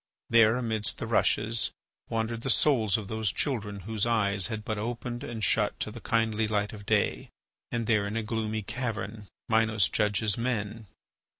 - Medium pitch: No, low, 110 Hz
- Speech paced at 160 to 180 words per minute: Yes, average, 170 wpm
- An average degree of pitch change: No, narrow, 1.6 semitones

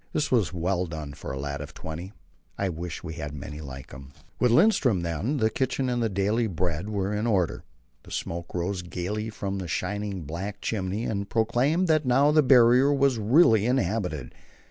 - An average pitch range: No, wide, 6.0 semitones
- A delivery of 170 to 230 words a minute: Yes, average, 190 wpm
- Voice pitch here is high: No, low, 100 Hz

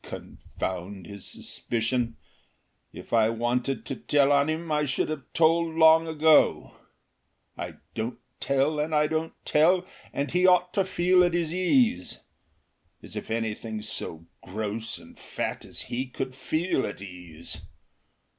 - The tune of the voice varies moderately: No, wide, 6.2 semitones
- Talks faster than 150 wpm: No, average, 145 wpm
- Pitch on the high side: No, medium, 140 Hz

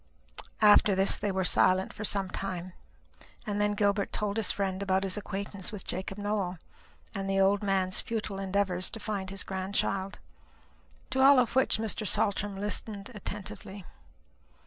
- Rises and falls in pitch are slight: Yes, narrow, 1.5 semitones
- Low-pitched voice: No, high, 200 Hz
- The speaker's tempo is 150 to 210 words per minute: Yes, average, 155 wpm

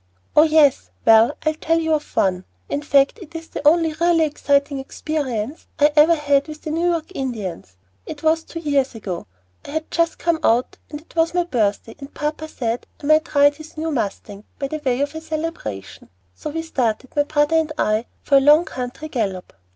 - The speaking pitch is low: No, very high, 295 Hz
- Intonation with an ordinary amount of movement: Yes, average, 4.1 semitones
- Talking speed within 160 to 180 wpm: No, average, 200 wpm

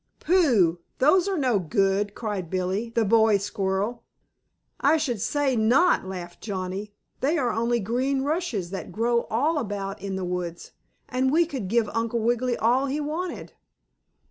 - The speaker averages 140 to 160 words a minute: Yes, average, 155 wpm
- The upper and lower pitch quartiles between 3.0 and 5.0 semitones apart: No, wide, 5.5 semitones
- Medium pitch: No, high, 230 Hz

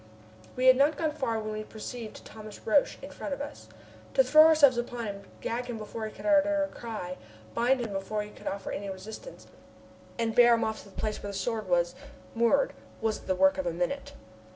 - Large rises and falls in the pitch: No, average, 4.4 semitones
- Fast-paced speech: Yes, fast, 220 wpm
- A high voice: Yes, high, 225 Hz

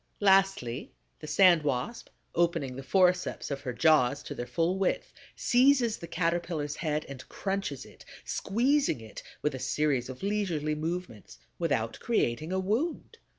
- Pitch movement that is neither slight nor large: No, wide, 5.8 semitones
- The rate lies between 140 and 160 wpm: Yes, average, 150 wpm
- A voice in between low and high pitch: Yes, medium, 165 Hz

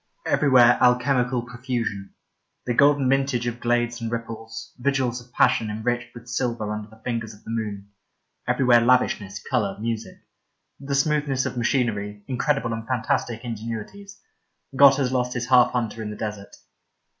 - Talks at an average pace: Yes, average, 155 wpm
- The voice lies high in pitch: No, low, 120 Hz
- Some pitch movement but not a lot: No, narrow, 2.3 semitones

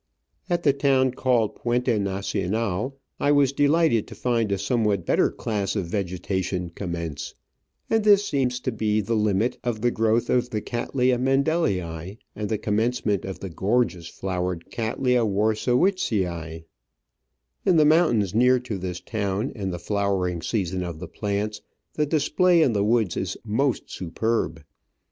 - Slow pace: No, average, 155 wpm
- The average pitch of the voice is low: Yes, low, 110 Hz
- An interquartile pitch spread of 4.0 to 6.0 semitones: Yes, average, 4.8 semitones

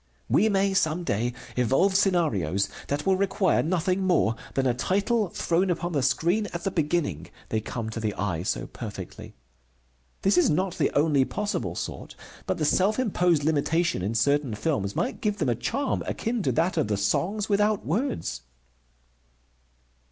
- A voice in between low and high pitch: Yes, medium, 165 Hz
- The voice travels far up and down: Yes, wide, 7.9 semitones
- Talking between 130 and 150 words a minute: No, average, 165 wpm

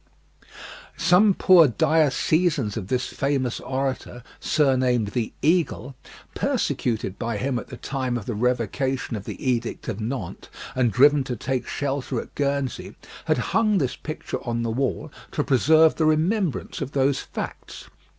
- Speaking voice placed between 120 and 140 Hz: Yes, low, 135 Hz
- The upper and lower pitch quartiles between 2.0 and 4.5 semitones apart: Yes, average, 3.7 semitones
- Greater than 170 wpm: No, average, 150 wpm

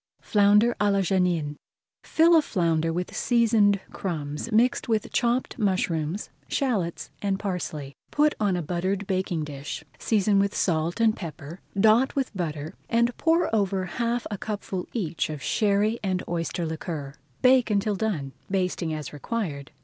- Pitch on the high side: Yes, high, 195 Hz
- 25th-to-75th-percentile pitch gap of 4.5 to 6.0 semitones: Yes, average, 4.9 semitones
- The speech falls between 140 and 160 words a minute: Yes, average, 150 wpm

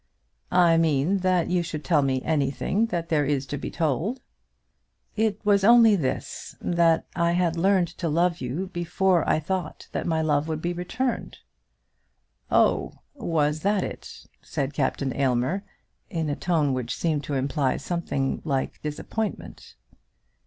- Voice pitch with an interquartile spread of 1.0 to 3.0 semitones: No, average, 3.8 semitones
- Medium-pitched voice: Yes, medium, 165 Hz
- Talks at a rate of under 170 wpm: Yes, average, 150 wpm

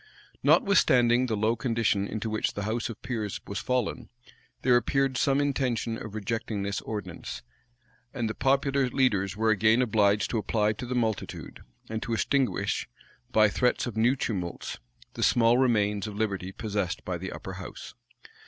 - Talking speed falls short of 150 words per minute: No, average, 160 wpm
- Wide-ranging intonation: No, average, 3.2 semitones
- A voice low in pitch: Yes, low, 110 Hz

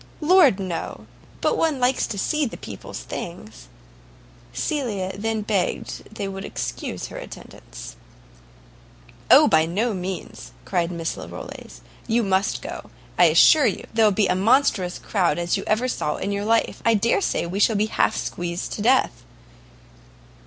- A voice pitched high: Yes, high, 200 Hz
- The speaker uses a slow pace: No, average, 160 wpm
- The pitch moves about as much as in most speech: Yes, average, 4.2 semitones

